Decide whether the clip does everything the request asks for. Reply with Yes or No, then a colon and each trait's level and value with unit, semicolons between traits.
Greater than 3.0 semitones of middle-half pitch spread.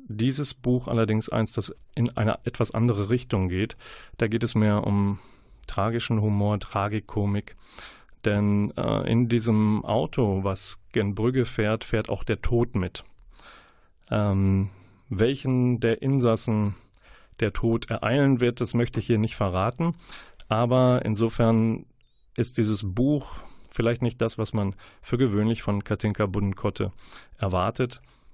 No: average, 2.7 semitones